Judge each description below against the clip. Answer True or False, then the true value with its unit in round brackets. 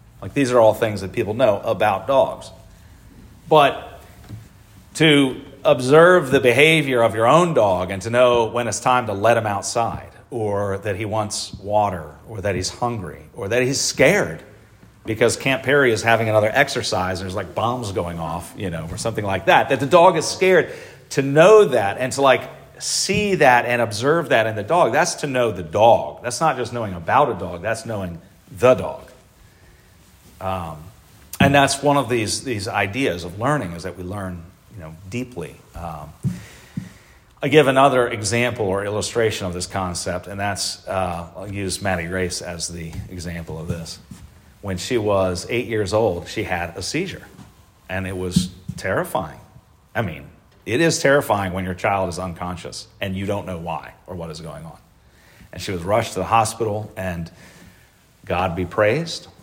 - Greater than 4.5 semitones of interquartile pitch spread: True (4.9 semitones)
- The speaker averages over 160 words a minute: True (180 wpm)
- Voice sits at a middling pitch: False (105 Hz)